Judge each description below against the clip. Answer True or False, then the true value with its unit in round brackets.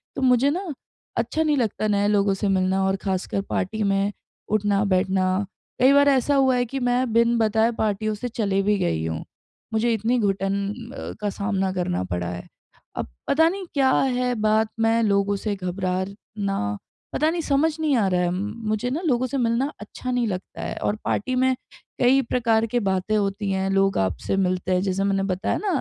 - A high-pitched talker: True (210 Hz)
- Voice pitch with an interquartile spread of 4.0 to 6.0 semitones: True (4.3 semitones)